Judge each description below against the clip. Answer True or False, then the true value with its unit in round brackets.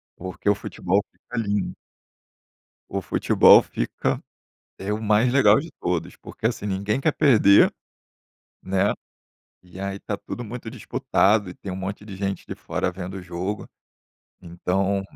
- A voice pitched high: False (100 Hz)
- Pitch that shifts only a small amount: True (2.2 semitones)